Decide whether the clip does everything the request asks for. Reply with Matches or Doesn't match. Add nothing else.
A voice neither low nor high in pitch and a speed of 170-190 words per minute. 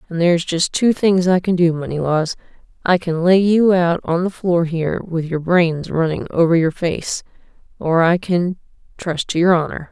Matches